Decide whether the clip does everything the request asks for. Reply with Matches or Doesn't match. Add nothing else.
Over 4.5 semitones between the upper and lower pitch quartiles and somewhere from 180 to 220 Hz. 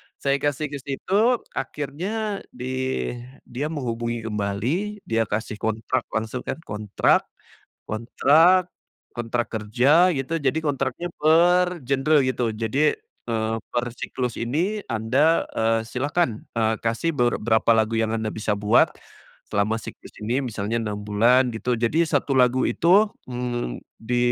Doesn't match